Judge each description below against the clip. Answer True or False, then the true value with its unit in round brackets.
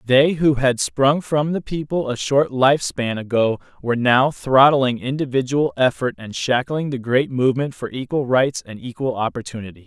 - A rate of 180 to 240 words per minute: False (170 wpm)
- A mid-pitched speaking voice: False (130 Hz)